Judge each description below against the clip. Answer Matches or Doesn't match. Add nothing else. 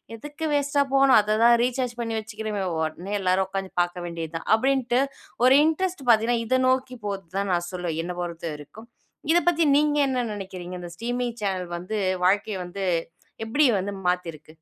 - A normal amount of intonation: Doesn't match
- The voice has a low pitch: Doesn't match